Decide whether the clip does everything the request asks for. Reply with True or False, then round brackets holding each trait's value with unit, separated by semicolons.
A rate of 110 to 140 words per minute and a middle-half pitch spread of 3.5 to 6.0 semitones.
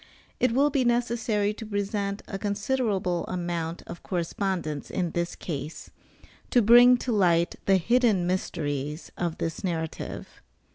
True (135 wpm; 4.9 semitones)